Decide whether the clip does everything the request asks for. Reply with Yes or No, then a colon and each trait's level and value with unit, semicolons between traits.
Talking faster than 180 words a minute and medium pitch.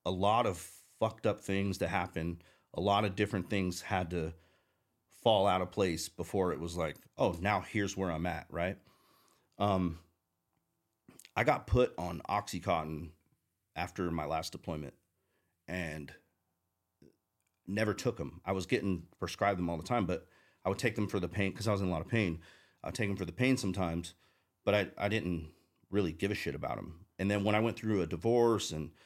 No: average, 195 wpm; very low, 95 Hz